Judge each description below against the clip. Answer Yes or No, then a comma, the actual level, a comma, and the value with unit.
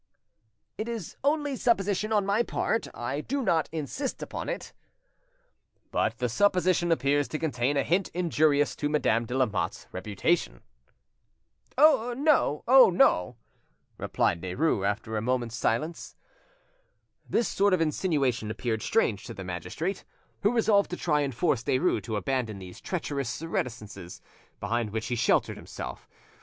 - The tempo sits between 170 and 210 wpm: No, average, 140 wpm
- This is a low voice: No, medium, 145 Hz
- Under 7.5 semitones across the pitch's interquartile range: No, wide, 8.9 semitones